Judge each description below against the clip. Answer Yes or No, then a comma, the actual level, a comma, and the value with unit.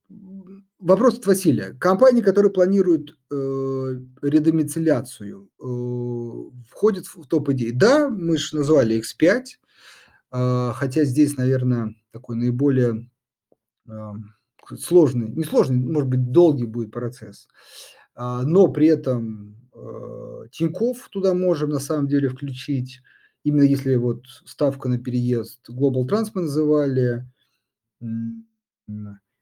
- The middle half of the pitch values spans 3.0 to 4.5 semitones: No, average, 5.0 semitones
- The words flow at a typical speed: No, slow, 100 wpm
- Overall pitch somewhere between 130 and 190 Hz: Yes, low, 135 Hz